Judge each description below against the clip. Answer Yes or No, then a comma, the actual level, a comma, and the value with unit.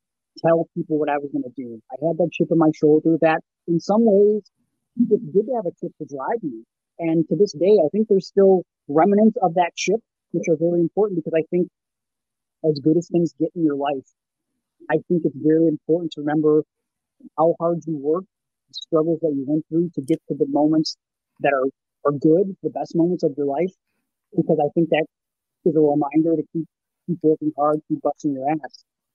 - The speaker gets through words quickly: Yes, fast, 210 wpm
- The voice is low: No, medium, 160 Hz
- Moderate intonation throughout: No, narrow, 2.1 semitones